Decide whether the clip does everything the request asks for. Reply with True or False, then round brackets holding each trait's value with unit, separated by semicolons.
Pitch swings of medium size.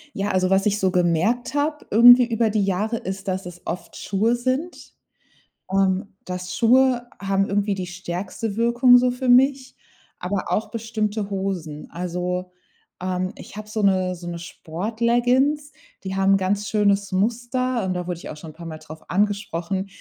True (4.3 semitones)